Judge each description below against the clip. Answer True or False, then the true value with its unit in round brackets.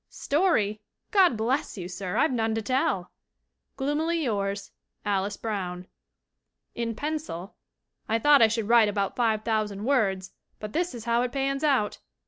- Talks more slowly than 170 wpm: True (150 wpm)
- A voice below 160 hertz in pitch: False (225 Hz)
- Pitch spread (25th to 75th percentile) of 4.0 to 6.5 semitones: True (5.2 semitones)